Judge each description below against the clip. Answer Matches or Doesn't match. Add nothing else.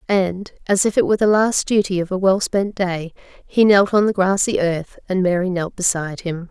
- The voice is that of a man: Doesn't match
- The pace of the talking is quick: Matches